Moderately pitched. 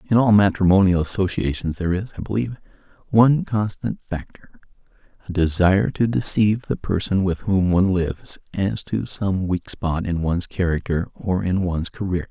No: very low, 95 Hz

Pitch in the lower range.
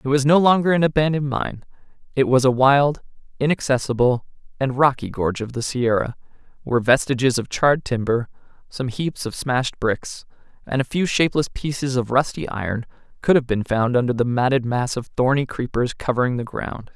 Yes: low, 130 Hz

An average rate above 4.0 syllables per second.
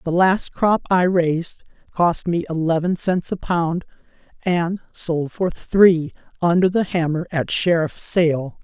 No: 3.8 syllables/s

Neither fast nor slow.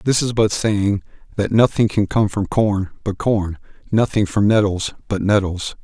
Yes: average, 175 wpm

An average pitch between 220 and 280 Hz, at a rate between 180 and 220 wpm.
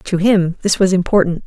No: medium, 185 Hz; fast, 205 wpm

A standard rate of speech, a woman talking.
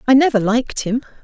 Yes: average, 195 wpm; female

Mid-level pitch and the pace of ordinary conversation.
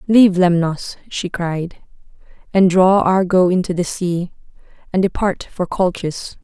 No: medium, 180 Hz; slow, 130 wpm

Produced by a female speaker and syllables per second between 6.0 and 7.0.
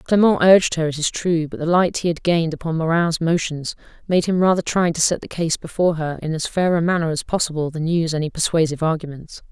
Yes: female; 6.2 syllables/s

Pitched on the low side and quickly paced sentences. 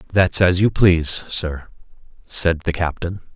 No: very low, 85 Hz; average, 145 wpm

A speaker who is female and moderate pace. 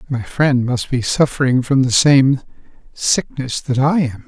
No: male; average, 170 wpm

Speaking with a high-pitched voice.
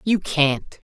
No: medium, 165 Hz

